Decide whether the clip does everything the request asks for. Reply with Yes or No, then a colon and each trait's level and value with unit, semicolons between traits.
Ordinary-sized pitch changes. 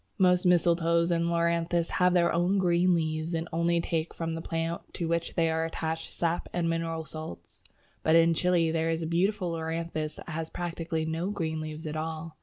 No: narrow, 1.0 semitones